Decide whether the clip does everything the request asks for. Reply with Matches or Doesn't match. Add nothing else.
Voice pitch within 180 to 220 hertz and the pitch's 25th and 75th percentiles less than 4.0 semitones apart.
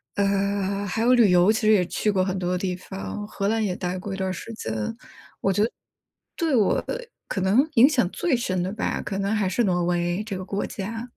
Matches